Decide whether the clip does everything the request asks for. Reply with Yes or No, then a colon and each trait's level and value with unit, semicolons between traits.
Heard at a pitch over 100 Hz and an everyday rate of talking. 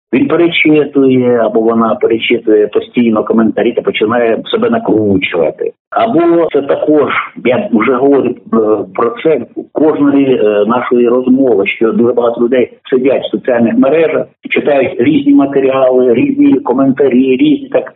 Yes: low, 135 Hz; average, 125 wpm